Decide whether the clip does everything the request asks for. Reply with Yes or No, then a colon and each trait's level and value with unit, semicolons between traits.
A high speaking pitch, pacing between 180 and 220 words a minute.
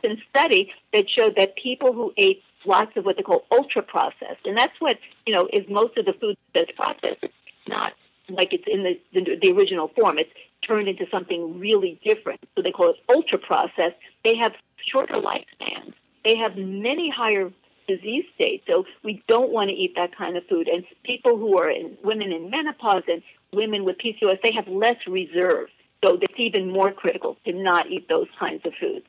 Yes: very high, 250 Hz; average, 200 wpm